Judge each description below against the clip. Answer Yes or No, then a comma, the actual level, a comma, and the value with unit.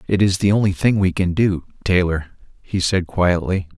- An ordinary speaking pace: Yes, average, 190 wpm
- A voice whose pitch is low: Yes, very low, 95 Hz